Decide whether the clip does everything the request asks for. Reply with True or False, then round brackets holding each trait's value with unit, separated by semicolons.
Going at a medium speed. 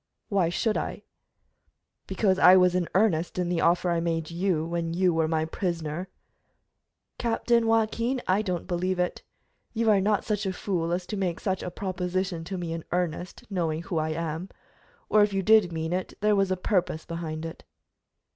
True (185 wpm)